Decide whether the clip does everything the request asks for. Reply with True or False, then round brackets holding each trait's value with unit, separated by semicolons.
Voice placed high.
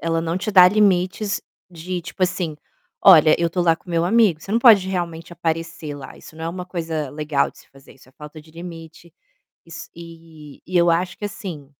False (170 Hz)